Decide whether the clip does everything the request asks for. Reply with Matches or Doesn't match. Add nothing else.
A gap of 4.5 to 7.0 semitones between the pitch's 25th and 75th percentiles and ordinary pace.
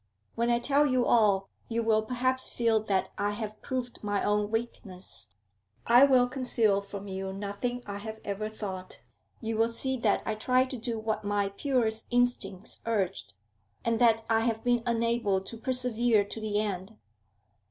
Doesn't match